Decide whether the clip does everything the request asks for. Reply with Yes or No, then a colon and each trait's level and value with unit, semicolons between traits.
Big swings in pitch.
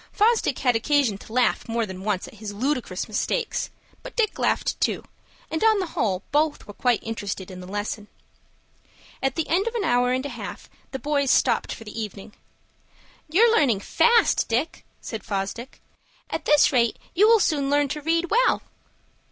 Yes: wide, 7.1 semitones